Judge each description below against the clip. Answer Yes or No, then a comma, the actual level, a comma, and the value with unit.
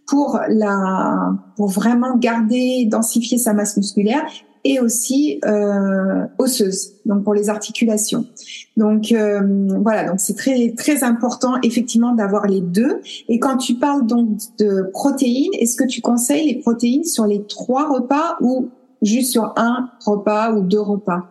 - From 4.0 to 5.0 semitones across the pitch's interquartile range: No, average, 3.4 semitones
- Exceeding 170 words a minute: No, average, 155 wpm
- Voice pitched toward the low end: No, high, 230 Hz